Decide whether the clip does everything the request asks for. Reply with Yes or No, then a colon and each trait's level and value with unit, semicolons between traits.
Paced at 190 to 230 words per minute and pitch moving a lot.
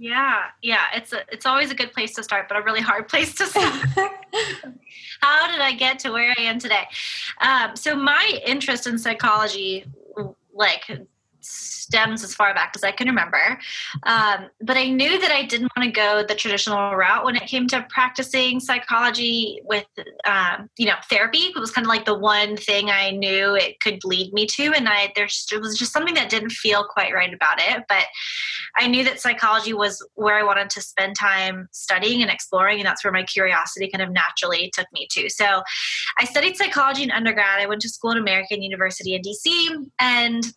No: fast, 205 wpm; average, 4.3 semitones